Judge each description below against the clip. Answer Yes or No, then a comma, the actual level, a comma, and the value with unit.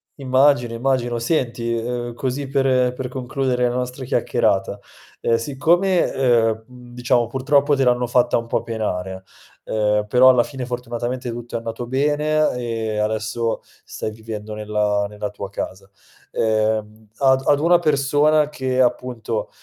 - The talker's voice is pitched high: No, low, 120 Hz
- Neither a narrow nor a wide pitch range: Yes, average, 3.0 semitones